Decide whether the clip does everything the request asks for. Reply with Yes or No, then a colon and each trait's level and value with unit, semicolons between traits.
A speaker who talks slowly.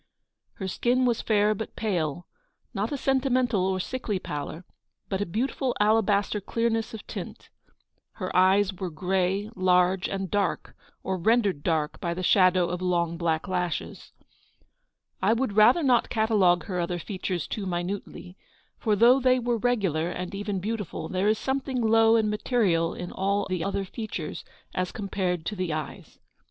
No: average, 165 wpm